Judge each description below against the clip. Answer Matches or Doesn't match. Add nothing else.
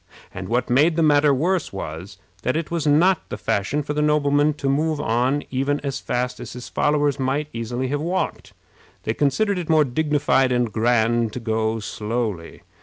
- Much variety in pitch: Doesn't match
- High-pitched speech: Doesn't match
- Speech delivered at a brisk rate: Doesn't match